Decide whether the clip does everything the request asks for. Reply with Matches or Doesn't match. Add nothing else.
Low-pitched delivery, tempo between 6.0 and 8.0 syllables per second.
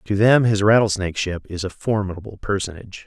Matches